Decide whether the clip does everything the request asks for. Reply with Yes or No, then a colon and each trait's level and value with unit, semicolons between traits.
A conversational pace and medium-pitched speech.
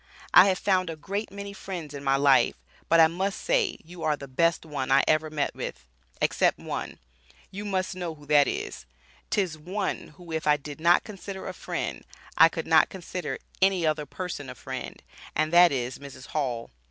Yes: average, 195 wpm; medium, 165 Hz